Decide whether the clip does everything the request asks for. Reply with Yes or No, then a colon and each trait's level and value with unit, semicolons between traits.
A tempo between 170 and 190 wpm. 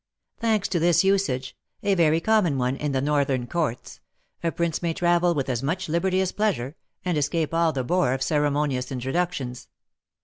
Yes: average, 175 wpm